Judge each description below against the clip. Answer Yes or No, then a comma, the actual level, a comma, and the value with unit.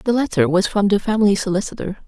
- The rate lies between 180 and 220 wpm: Yes, average, 200 wpm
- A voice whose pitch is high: Yes, high, 205 Hz